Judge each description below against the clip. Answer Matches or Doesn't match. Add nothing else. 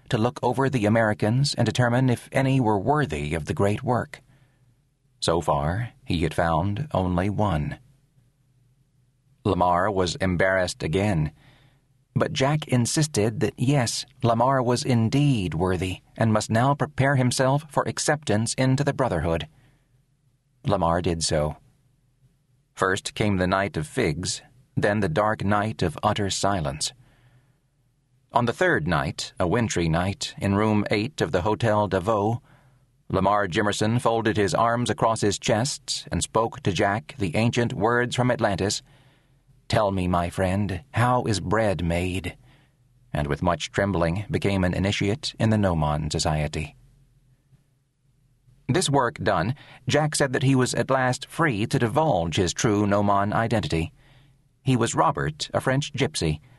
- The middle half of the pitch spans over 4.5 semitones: Matches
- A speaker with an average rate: Matches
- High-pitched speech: Doesn't match